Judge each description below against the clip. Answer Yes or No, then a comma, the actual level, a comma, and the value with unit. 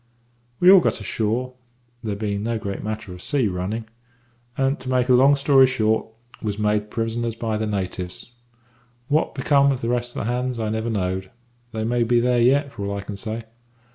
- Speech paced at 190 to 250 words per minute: Yes, average, 200 wpm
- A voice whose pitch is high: No, low, 115 Hz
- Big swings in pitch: No, average, 3.2 semitones